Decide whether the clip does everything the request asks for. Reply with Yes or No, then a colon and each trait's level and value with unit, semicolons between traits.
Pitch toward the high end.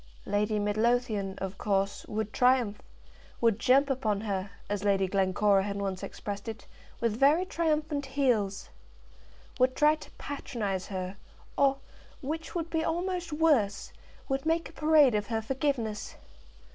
Yes: high, 230 Hz